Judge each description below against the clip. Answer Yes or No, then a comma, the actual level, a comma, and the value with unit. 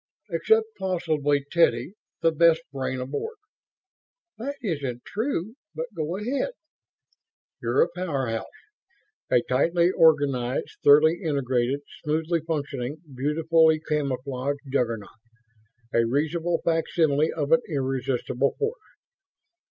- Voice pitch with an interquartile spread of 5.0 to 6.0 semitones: No, average, 4.0 semitones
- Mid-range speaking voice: Yes, medium, 155 Hz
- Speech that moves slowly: Yes, slow, 100 wpm